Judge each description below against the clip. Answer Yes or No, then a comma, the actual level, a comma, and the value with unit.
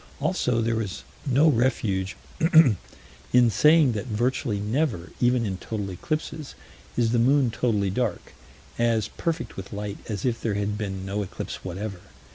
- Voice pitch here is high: No, low, 115 Hz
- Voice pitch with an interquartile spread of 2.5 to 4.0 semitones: Yes, average, 3.7 semitones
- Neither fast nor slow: Yes, average, 150 wpm